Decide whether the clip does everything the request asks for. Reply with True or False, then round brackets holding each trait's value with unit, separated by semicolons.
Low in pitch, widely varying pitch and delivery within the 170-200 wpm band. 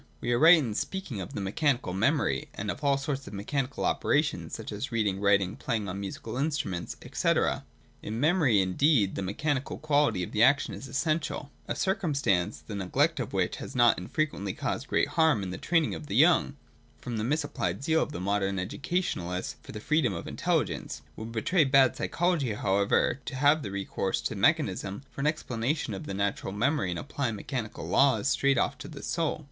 True (120 Hz; 6.8 semitones; 190 wpm)